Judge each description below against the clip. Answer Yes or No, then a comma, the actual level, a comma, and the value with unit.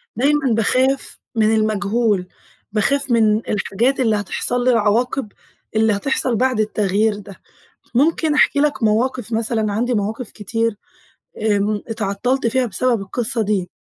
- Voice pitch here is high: Yes, high, 225 Hz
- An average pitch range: Yes, average, 3.3 semitones